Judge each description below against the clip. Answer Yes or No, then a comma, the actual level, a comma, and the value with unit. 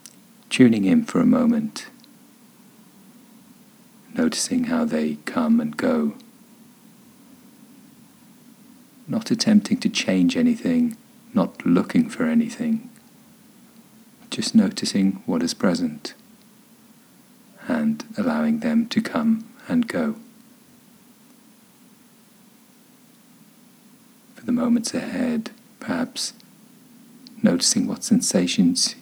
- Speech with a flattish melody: Yes, narrow, 1.3 semitones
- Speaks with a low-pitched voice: No, high, 235 Hz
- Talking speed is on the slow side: Yes, slow, 85 wpm